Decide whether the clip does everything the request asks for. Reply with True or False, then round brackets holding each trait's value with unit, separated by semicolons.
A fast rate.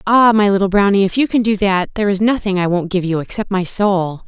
True (265 wpm)